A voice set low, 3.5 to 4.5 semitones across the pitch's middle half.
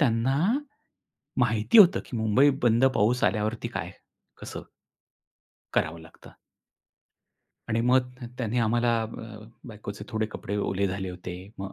No: low, 110 Hz; average, 2.8 semitones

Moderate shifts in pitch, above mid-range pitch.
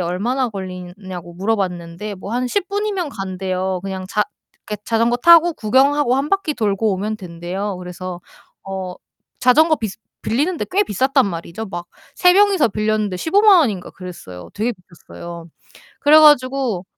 No: wide, 7.0 semitones; high, 210 Hz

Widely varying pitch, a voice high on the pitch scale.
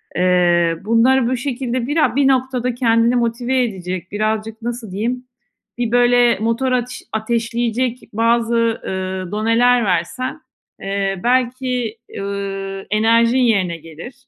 No: average, 3.8 semitones; high, 230 Hz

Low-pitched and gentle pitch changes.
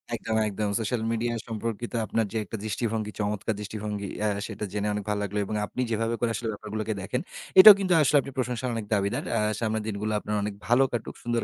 Yes: low, 110 Hz; narrow, 2.0 semitones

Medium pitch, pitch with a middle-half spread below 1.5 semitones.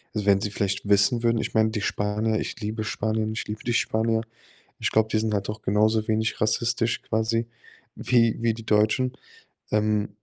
No: low, 110 Hz; narrow, 1.1 semitones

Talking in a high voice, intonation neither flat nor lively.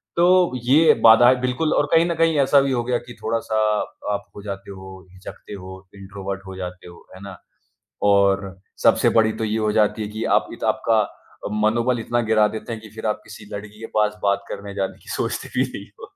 No: low, 105 Hz; average, 3.4 semitones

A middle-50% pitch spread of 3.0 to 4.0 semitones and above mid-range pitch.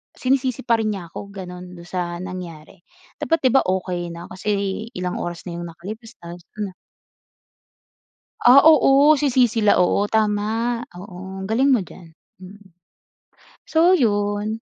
No: average, 4.5 semitones; high, 205 Hz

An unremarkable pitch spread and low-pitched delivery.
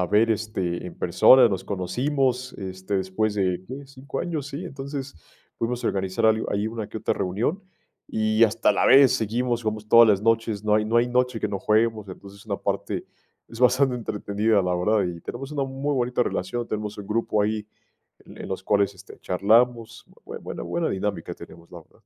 Yes: average, 3.7 semitones; low, 110 Hz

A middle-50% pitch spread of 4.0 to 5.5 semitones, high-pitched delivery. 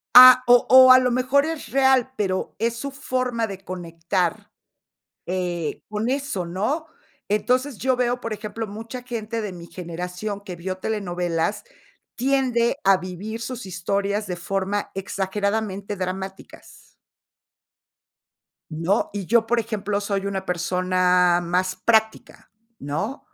Yes: average, 4.6 semitones; high, 205 Hz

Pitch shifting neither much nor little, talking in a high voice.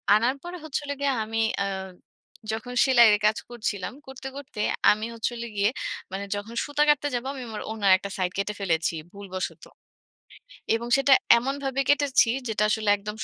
Yes: average, 4.8 semitones; high, 225 Hz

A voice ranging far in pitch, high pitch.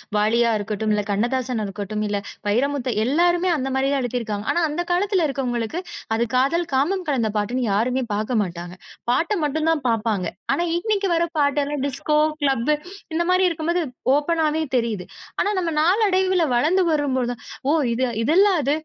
Yes: wide, 6.6 semitones; very high, 270 Hz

